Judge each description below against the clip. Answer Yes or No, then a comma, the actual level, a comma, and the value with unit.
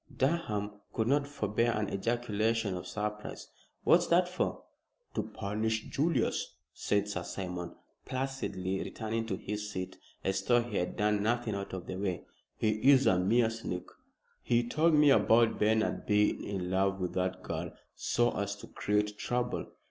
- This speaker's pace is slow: No, average, 160 wpm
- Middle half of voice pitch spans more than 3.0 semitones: Yes, average, 3.5 semitones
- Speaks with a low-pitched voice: Yes, low, 105 Hz